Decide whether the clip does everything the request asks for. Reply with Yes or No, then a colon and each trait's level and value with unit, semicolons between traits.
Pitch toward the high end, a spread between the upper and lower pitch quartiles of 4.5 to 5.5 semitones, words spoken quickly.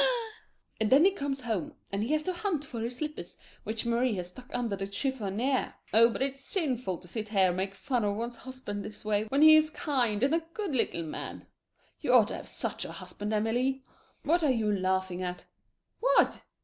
Yes: high, 235 Hz; average, 5.2 semitones; fast, 210 wpm